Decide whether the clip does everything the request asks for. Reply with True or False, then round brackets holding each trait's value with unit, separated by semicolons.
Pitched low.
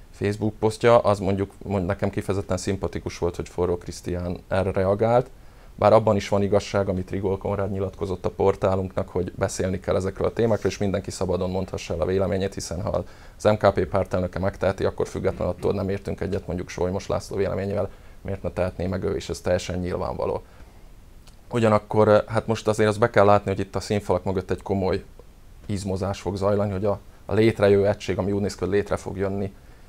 True (100 Hz)